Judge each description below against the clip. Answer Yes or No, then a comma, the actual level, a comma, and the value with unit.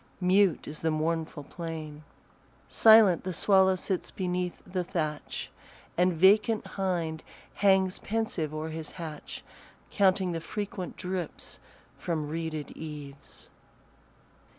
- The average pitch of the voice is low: No, medium, 175 Hz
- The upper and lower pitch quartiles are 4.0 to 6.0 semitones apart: No, average, 3.3 semitones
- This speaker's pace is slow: Yes, slow, 110 wpm